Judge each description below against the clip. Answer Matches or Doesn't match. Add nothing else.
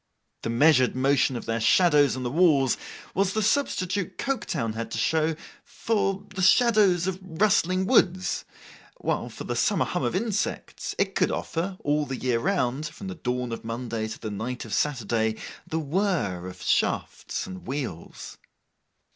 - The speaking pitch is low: Doesn't match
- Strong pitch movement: Matches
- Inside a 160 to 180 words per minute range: Matches